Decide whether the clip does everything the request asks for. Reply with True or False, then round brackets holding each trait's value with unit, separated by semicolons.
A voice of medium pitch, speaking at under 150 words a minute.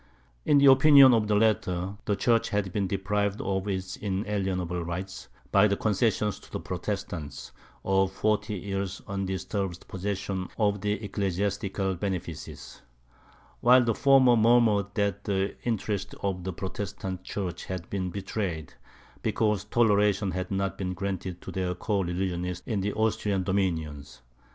False (100 Hz; 140 wpm)